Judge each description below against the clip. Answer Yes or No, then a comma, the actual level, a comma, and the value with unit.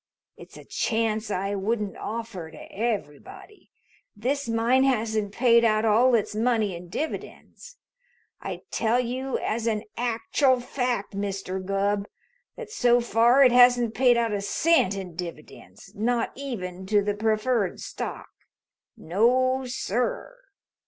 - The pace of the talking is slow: Yes, slow, 130 wpm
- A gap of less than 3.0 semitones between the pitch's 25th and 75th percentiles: No, average, 3.5 semitones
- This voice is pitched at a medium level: No, high, 225 Hz